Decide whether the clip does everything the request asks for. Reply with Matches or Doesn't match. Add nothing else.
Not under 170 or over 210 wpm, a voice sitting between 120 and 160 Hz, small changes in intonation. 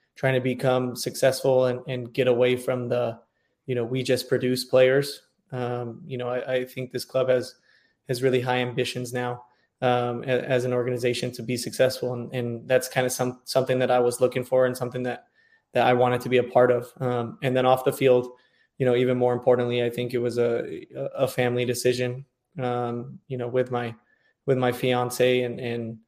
Matches